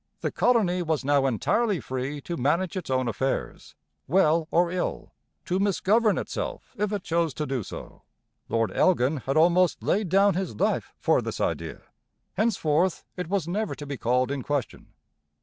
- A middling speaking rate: Yes, average, 165 wpm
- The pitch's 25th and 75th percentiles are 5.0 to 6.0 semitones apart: Yes, wide, 5.6 semitones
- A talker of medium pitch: Yes, medium, 170 Hz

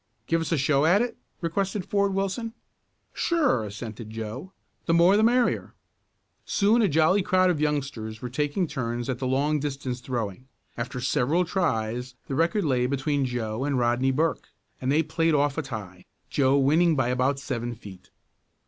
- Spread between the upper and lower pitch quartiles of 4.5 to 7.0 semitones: Yes, wide, 5.4 semitones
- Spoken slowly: No, average, 170 wpm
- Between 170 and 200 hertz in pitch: No, medium, 140 Hz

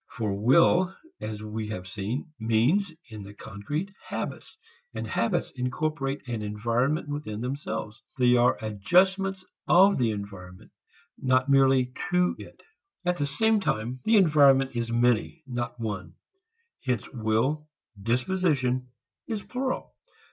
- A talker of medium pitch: No, low, 125 Hz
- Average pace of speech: No, slow, 125 wpm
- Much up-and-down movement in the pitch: Yes, wide, 5.9 semitones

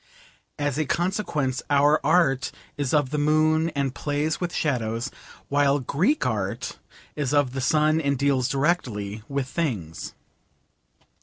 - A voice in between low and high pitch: Yes, medium, 145 Hz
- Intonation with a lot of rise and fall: No, average, 2.9 semitones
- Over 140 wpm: No, slow, 135 wpm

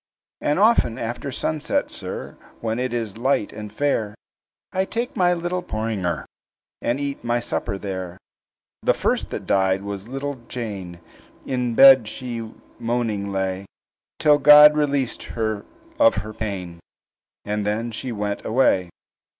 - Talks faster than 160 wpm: No, average, 140 wpm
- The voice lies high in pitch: No, low, 115 Hz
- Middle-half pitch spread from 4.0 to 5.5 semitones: Yes, average, 5.1 semitones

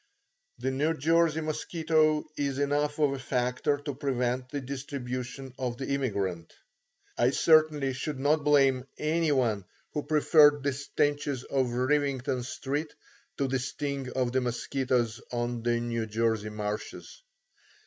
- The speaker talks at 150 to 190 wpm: No, average, 140 wpm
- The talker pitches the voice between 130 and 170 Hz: Yes, low, 135 Hz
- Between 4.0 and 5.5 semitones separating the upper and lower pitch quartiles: No, average, 3.1 semitones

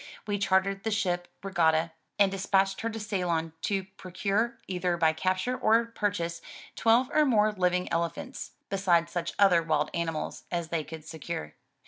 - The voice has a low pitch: No, medium, 185 Hz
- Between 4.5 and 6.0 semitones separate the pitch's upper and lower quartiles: No, average, 3.4 semitones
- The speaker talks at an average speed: Yes, average, 155 wpm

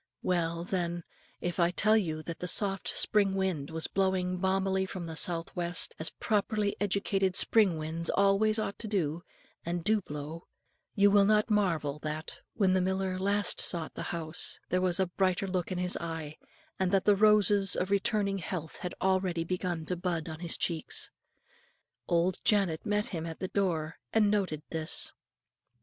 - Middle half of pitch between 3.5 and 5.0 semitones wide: No, average, 3.0 semitones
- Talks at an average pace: Yes, average, 175 wpm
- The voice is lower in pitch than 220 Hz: Yes, medium, 185 Hz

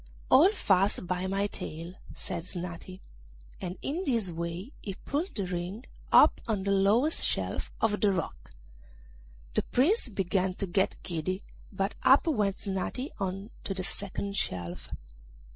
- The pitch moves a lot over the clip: No, average, 3.1 semitones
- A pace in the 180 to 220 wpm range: No, average, 145 wpm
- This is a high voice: Yes, high, 195 Hz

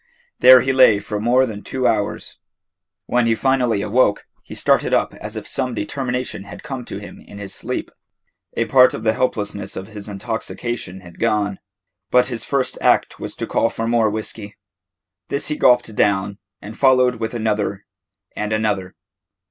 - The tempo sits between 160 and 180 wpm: Yes, average, 170 wpm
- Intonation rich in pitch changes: No, average, 3.4 semitones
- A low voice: Yes, low, 110 Hz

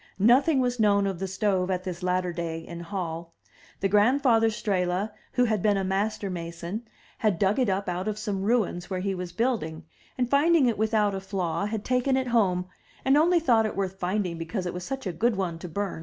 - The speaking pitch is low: No, high, 200 Hz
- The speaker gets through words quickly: Yes, fast, 215 wpm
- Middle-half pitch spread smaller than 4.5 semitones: Yes, average, 3.8 semitones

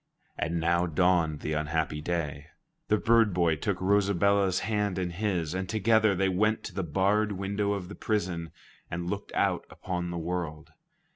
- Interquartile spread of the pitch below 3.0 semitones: No, average, 3.3 semitones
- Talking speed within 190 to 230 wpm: No, average, 165 wpm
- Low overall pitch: Yes, very low, 90 Hz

